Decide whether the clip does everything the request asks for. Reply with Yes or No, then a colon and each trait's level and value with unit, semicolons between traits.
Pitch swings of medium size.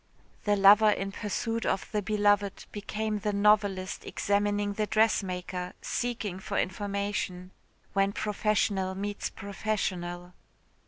No: narrow, 1.7 semitones